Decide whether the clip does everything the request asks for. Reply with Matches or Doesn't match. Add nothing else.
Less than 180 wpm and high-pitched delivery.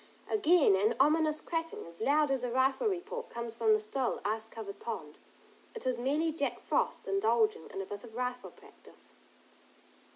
Matches